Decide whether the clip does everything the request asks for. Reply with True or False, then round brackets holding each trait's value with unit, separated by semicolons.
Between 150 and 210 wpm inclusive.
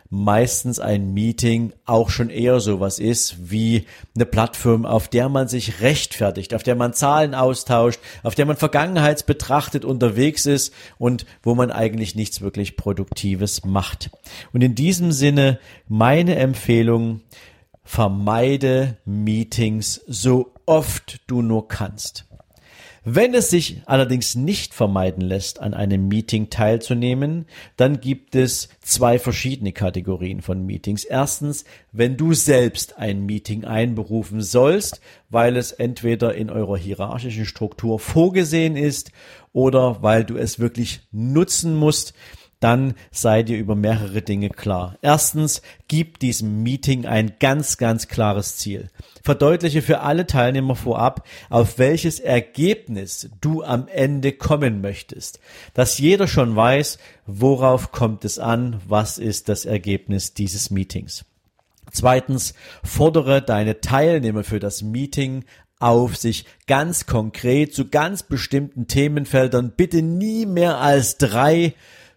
False (130 wpm)